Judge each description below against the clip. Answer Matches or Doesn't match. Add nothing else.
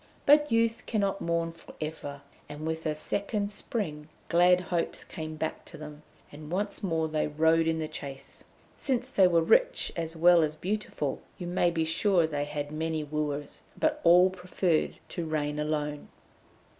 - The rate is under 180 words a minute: Matches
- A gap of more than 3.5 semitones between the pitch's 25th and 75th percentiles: Doesn't match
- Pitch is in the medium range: Matches